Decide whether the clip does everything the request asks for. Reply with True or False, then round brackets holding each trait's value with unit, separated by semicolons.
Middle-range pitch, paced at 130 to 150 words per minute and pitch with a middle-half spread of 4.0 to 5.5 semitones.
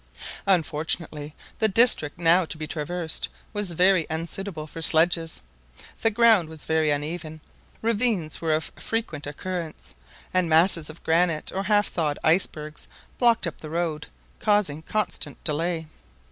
False (165 Hz; 135 wpm; 3.5 semitones)